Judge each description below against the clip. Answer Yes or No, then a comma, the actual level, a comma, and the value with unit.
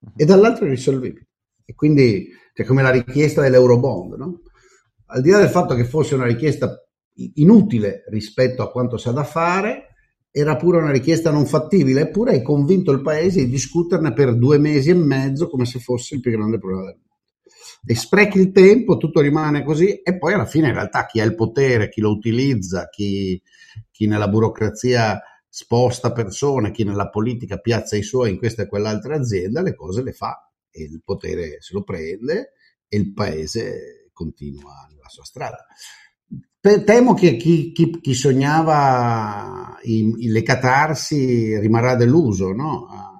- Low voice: Yes, low, 125 Hz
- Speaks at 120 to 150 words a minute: No, fast, 170 wpm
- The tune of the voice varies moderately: No, wide, 5.8 semitones